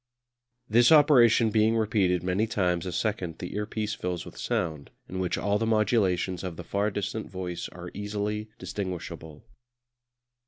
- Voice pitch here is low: Yes, low, 100 Hz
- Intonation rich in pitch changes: No, average, 3.2 semitones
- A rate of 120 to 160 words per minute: Yes, average, 150 wpm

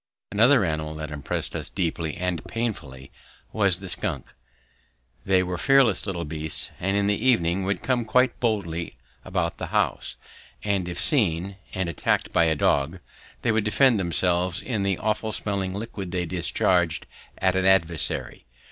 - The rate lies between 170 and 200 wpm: No, average, 155 wpm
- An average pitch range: Yes, average, 3.8 semitones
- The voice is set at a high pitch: No, very low, 95 Hz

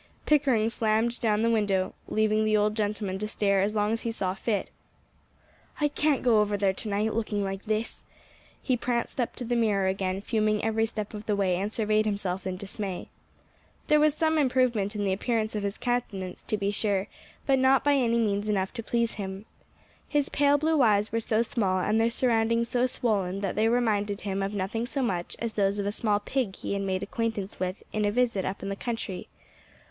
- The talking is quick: Yes, fast, 210 wpm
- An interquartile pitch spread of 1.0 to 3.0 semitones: Yes, average, 2.7 semitones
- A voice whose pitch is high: Yes, high, 215 Hz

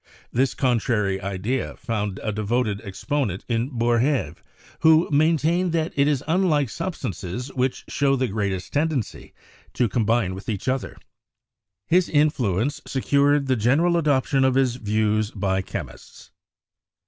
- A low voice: Yes, low, 125 Hz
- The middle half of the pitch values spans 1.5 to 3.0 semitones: No, average, 5.3 semitones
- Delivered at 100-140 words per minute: Yes, slow, 135 wpm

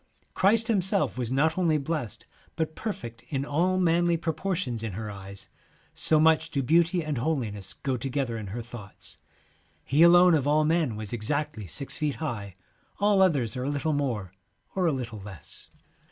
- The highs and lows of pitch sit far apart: Yes, wide, 6.1 semitones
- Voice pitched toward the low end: No, medium, 145 Hz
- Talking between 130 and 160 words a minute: No, average, 180 wpm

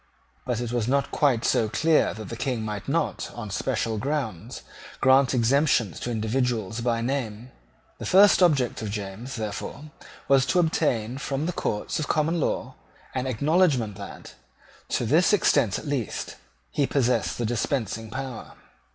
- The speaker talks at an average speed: Yes, average, 155 wpm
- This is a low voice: Yes, low, 125 Hz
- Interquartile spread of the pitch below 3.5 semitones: No, average, 4.2 semitones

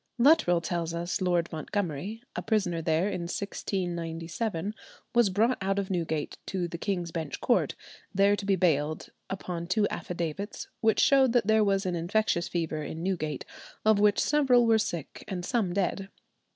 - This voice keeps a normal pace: Yes, average, 165 wpm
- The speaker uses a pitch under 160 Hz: No, medium, 185 Hz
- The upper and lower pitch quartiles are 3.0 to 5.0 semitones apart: Yes, average, 3.6 semitones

